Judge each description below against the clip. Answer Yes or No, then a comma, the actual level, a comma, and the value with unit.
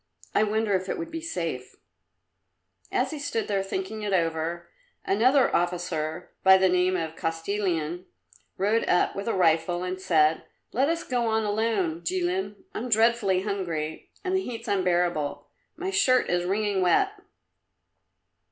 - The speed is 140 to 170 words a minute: Yes, average, 150 wpm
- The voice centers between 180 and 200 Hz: Yes, high, 190 Hz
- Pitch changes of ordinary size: Yes, average, 4.4 semitones